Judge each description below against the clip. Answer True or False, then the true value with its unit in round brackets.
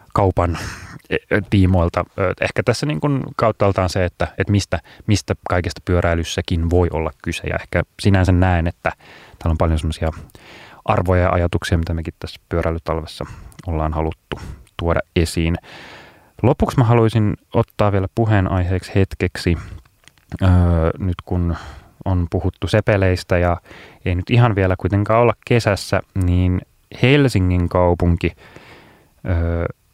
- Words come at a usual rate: True (120 wpm)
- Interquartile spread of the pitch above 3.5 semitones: False (2.9 semitones)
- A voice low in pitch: True (90 Hz)